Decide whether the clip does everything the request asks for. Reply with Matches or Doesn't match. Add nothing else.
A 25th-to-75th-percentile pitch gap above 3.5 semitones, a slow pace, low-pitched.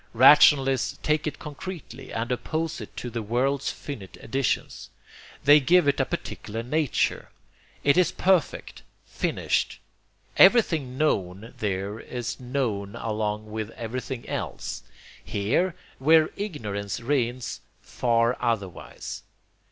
Matches